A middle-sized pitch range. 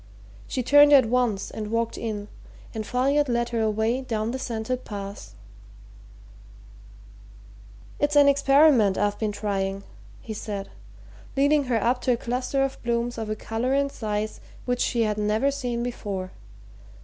Yes: average, 3.4 semitones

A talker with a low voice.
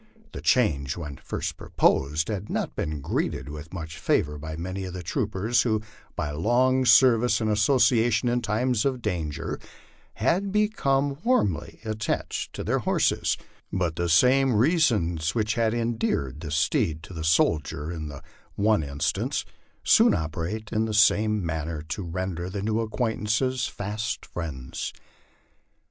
Yes: low, 105 Hz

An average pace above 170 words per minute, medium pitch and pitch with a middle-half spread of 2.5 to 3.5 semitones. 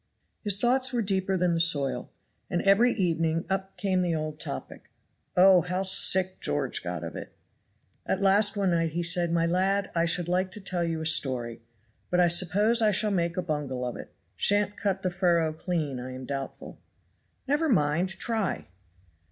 Yes: average, 185 wpm; medium, 180 Hz; average, 3.1 semitones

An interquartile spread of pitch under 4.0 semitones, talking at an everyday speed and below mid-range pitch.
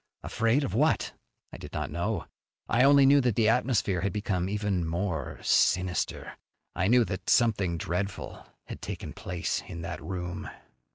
No: average, 4.8 semitones; average, 160 wpm; low, 100 Hz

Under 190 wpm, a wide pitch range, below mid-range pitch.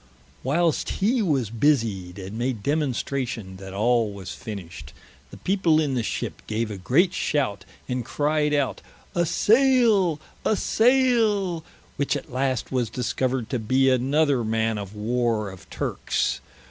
Yes: average, 145 wpm; wide, 6.1 semitones; low, 130 Hz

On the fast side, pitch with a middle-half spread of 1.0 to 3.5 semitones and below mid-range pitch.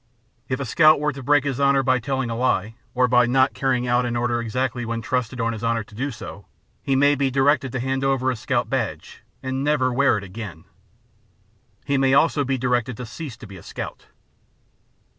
Yes: fast, 215 wpm; narrow, 2.6 semitones; low, 130 Hz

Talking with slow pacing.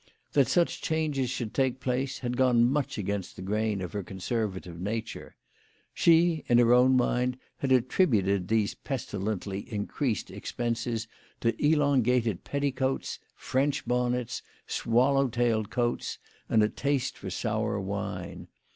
Yes: slow, 130 wpm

